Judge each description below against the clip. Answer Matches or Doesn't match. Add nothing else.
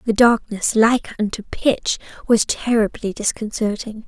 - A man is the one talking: Doesn't match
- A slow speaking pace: Matches